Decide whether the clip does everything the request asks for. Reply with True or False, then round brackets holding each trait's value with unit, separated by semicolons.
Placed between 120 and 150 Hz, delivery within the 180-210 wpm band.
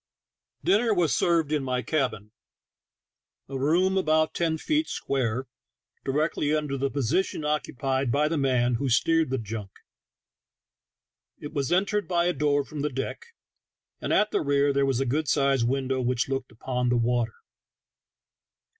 False (140 Hz; 160 wpm)